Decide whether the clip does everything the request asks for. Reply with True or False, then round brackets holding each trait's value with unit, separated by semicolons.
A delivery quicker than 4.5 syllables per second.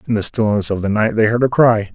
True (6.2 syllables/s)